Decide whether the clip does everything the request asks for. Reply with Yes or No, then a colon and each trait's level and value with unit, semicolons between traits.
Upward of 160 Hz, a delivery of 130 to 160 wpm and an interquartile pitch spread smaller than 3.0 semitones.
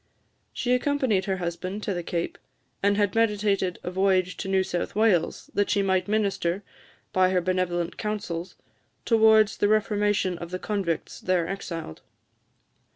Yes: high, 190 Hz; average, 150 wpm; narrow, 2.6 semitones